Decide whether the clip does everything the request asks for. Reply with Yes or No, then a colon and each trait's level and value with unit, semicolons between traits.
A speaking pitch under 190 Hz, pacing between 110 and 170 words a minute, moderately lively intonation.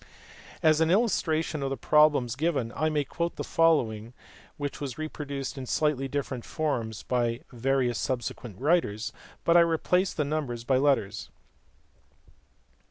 Yes: medium, 140 Hz; average, 145 wpm; average, 4.2 semitones